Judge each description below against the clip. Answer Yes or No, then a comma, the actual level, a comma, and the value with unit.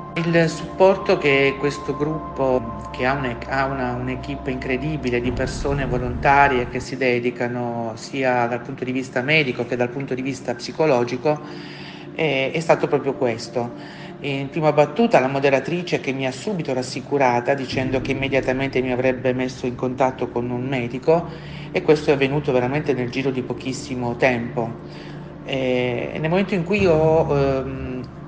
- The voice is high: No, low, 135 Hz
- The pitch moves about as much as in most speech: Yes, average, 3.0 semitones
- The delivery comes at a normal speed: Yes, average, 150 wpm